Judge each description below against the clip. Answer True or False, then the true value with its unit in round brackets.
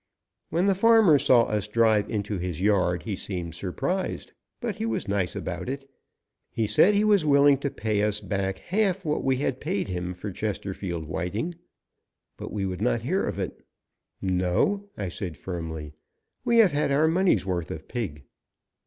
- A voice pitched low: True (105 Hz)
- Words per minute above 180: False (175 wpm)